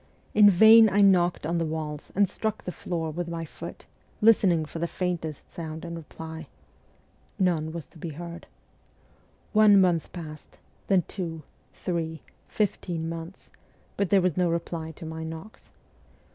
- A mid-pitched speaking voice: Yes, medium, 170 Hz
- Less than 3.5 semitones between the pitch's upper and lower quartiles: Yes, narrow, 2.5 semitones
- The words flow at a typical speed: Yes, average, 155 wpm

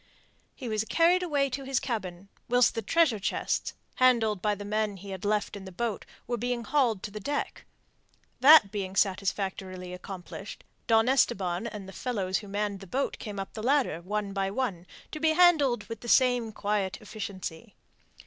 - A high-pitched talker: Yes, high, 215 Hz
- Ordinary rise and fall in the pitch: Yes, average, 4.1 semitones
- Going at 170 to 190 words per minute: Yes, average, 185 wpm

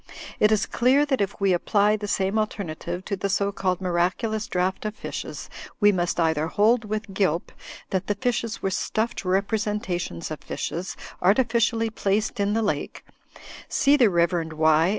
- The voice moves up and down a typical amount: Yes, average, 3.3 semitones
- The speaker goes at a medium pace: Yes, average, 165 wpm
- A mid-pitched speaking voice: No, high, 200 Hz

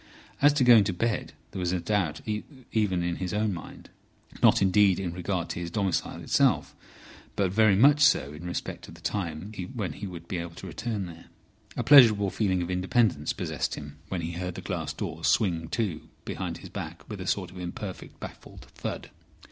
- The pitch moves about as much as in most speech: Yes, average, 3.4 semitones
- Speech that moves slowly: No, average, 195 wpm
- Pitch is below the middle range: Yes, very low, 95 Hz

